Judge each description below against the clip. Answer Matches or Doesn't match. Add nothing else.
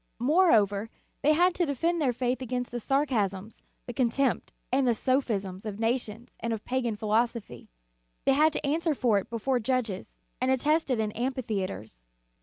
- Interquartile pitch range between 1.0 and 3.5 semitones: Doesn't match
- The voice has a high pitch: Matches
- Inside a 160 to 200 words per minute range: Matches